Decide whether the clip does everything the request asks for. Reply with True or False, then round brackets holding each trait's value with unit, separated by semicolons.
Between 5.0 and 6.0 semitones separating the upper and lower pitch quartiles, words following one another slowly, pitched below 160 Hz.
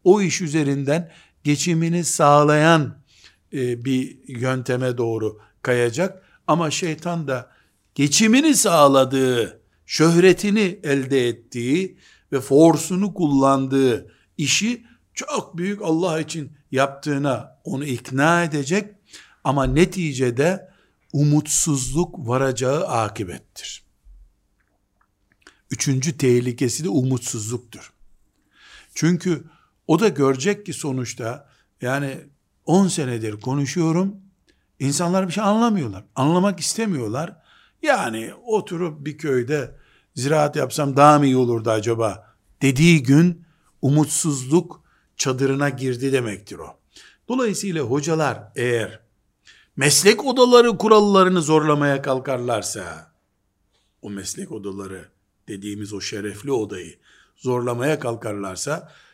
True (5.4 semitones; 90 wpm; 140 Hz)